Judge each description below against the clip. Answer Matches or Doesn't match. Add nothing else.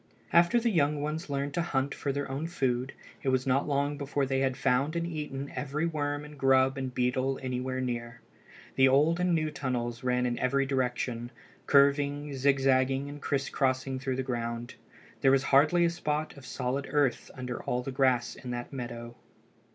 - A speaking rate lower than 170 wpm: Doesn't match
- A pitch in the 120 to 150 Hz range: Matches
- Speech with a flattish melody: Matches